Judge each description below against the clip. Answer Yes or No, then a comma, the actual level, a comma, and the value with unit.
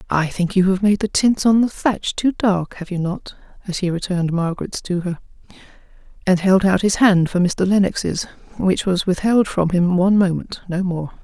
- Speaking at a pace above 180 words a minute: Yes, fast, 205 wpm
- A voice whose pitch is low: No, medium, 185 Hz